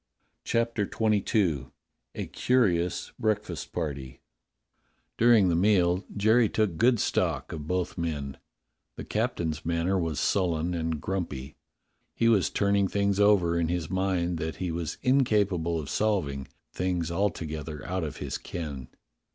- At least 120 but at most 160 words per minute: Yes, average, 140 wpm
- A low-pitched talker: Yes, very low, 90 Hz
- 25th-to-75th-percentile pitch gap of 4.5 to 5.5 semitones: No, average, 4.1 semitones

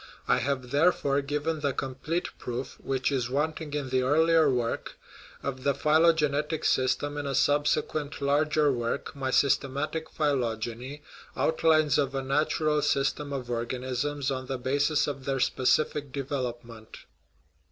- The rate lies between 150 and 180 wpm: No, average, 140 wpm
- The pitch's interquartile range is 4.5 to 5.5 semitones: No, narrow, 2.4 semitones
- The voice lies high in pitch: No, medium, 140 Hz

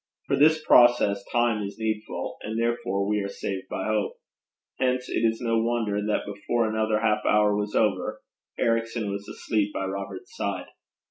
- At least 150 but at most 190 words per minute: Yes, average, 165 wpm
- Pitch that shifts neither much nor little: No, narrow, 2.1 semitones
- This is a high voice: No, low, 110 Hz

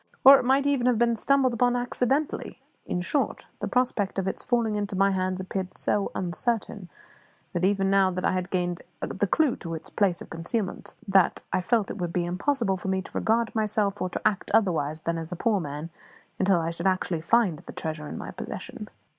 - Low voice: No, high, 195 Hz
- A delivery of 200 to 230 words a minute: Yes, fast, 205 wpm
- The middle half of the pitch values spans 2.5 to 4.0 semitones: No, average, 4.6 semitones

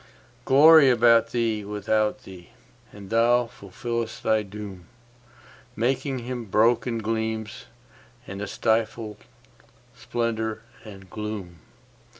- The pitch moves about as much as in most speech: No, narrow, 2.2 semitones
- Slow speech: Yes, slow, 95 wpm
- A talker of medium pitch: No, low, 110 Hz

